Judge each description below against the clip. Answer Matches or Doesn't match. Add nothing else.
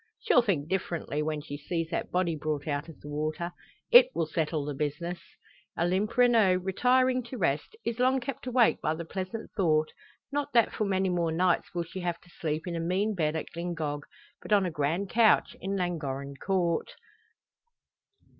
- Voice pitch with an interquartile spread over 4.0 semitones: Matches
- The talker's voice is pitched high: Doesn't match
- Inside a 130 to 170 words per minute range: Doesn't match